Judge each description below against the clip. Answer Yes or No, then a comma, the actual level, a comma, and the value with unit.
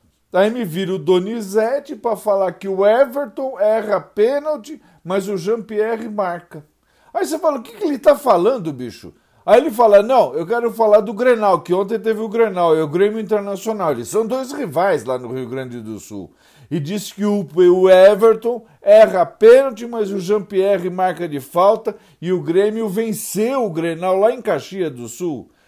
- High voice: Yes, high, 205 Hz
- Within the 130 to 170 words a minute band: No, average, 180 wpm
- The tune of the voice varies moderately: Yes, average, 4.3 semitones